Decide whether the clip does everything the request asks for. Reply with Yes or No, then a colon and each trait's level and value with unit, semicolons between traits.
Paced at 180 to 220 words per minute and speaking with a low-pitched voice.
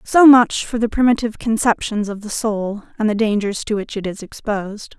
No: fast, 205 wpm; high, 215 Hz